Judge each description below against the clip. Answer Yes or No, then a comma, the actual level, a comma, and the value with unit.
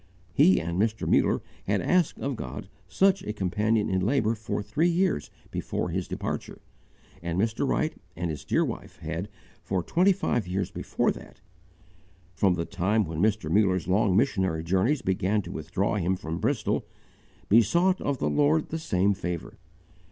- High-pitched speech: No, low, 100 Hz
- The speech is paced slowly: No, average, 165 wpm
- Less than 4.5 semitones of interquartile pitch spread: No, wide, 5.4 semitones